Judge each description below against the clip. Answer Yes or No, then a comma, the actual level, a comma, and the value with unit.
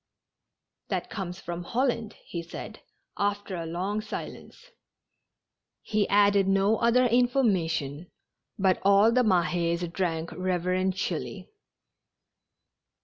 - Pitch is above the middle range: Yes, high, 195 Hz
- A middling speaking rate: No, slow, 100 wpm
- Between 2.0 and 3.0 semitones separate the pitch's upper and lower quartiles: No, average, 3.5 semitones